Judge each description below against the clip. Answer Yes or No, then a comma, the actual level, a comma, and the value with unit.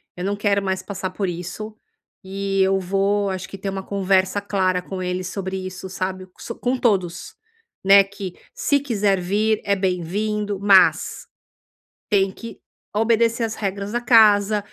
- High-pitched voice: Yes, high, 195 Hz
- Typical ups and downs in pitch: No, narrow, 1.7 semitones